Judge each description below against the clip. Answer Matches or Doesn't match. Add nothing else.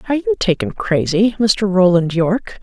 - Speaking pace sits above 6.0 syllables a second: Doesn't match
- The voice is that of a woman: Matches